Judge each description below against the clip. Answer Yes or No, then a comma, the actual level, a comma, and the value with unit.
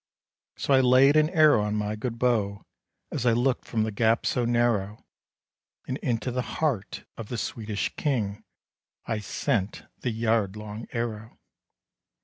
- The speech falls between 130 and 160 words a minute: Yes, average, 150 wpm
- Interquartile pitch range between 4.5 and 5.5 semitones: No, average, 2.9 semitones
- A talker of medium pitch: No, low, 115 Hz